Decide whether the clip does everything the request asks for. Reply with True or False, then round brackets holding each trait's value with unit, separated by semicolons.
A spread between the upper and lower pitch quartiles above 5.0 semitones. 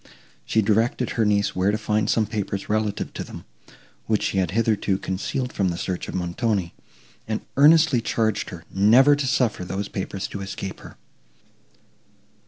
False (2.9 semitones)